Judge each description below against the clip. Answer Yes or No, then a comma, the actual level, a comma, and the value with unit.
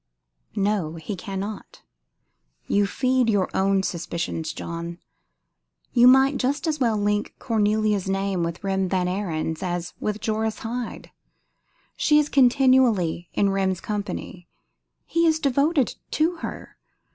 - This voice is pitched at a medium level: No, high, 205 Hz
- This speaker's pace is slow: Yes, slow, 125 wpm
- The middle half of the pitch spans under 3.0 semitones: No, average, 5.3 semitones